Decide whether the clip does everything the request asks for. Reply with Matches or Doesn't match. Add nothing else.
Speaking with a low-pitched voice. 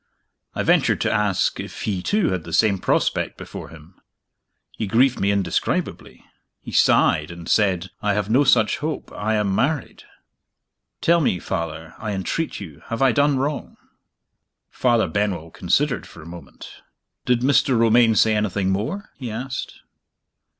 Matches